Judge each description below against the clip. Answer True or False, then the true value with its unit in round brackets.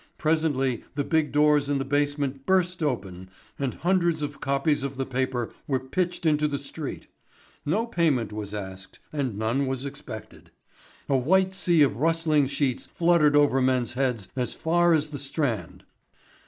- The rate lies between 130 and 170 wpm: True (160 wpm)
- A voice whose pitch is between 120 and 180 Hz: True (140 Hz)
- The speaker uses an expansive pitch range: False (3.4 semitones)